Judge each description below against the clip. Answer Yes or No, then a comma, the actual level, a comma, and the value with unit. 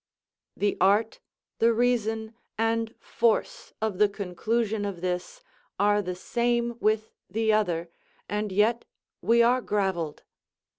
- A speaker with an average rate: No, slow, 120 wpm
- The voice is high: Yes, high, 215 Hz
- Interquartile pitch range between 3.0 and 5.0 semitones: No, narrow, 2.5 semitones